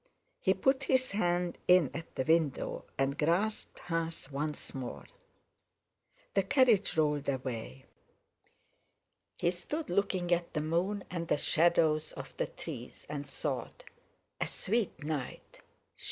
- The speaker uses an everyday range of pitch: Yes, average, 4.3 semitones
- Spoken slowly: Yes, slow, 125 wpm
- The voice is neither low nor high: Yes, medium, 170 Hz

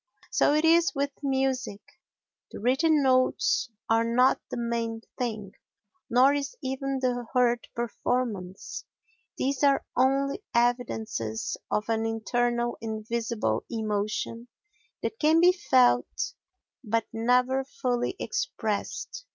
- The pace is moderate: No, slow, 110 wpm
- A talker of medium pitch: No, high, 245 Hz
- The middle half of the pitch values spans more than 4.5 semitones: No, average, 3.2 semitones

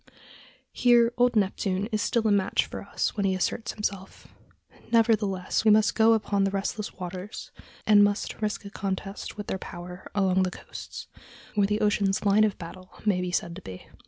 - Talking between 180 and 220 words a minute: Yes, average, 185 wpm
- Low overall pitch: No, high, 200 Hz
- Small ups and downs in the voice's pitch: Yes, narrow, 2.3 semitones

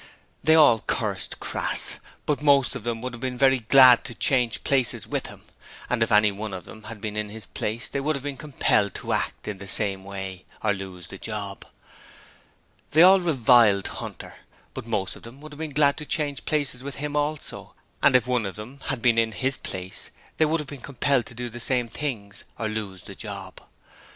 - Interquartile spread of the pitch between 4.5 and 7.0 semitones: Yes, average, 4.9 semitones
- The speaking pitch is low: Yes, low, 120 Hz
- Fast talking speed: Yes, fast, 215 wpm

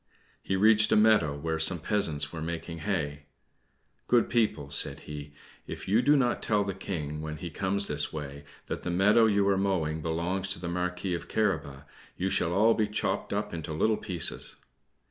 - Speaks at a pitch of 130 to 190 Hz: No, very low, 90 Hz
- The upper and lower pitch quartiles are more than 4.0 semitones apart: Yes, average, 4.7 semitones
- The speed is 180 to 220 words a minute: Yes, average, 185 wpm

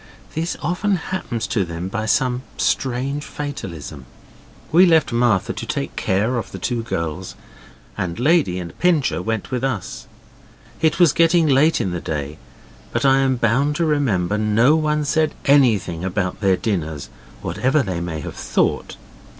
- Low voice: Yes, low, 120 Hz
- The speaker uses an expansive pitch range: Yes, wide, 8.2 semitones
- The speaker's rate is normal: Yes, average, 160 wpm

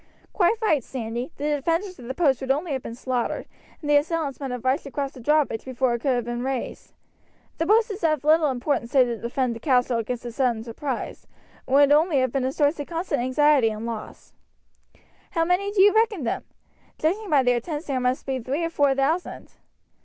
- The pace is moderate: No, fast, 215 wpm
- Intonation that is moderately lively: Yes, average, 4.0 semitones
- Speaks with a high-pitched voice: Yes, very high, 275 Hz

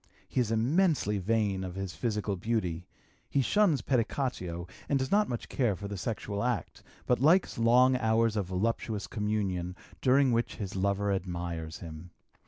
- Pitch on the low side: Yes, low, 105 Hz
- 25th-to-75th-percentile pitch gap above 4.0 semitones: Yes, average, 4.7 semitones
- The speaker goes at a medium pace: Yes, average, 160 wpm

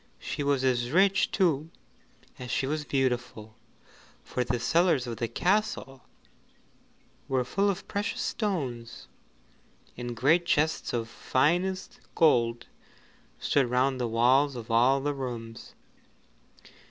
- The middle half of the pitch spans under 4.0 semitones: No, average, 4.8 semitones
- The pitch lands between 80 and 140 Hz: Yes, low, 135 Hz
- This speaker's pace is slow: Yes, slow, 125 wpm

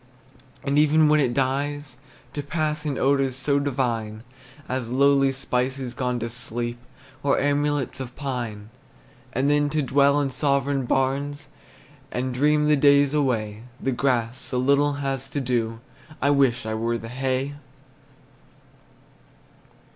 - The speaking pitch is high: No, low, 135 Hz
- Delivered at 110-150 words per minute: Yes, average, 140 wpm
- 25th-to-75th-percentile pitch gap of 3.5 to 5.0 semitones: No, narrow, 2.4 semitones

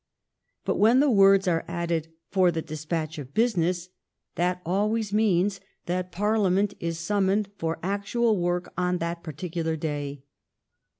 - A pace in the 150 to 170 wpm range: No, average, 140 wpm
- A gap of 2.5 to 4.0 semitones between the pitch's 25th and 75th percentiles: Yes, average, 3.4 semitones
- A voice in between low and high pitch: Yes, medium, 180 Hz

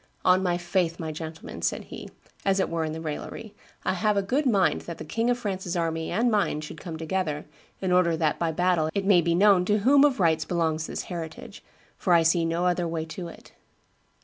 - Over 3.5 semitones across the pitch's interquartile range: No, average, 3.2 semitones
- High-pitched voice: No, medium, 175 Hz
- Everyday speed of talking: No, fast, 220 wpm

